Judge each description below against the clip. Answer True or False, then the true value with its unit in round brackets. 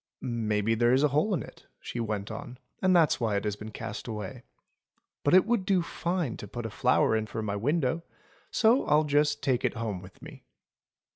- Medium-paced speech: False (210 wpm)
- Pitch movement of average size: False (6.3 semitones)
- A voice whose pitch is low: True (120 Hz)